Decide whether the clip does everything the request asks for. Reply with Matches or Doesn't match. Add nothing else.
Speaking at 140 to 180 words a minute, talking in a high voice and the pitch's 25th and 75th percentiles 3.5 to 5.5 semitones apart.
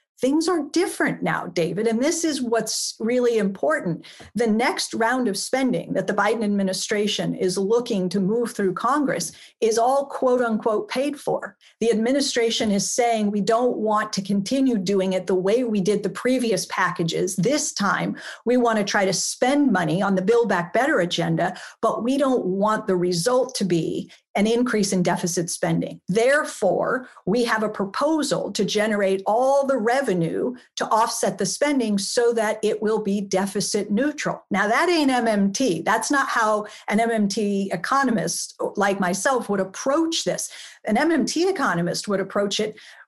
Matches